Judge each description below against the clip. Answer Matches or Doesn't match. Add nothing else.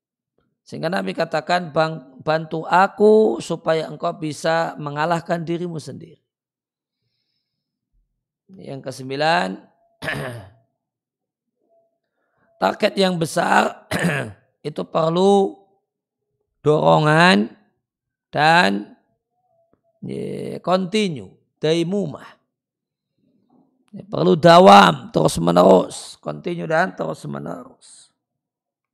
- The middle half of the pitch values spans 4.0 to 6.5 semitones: Matches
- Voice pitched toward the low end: Doesn't match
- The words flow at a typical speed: Doesn't match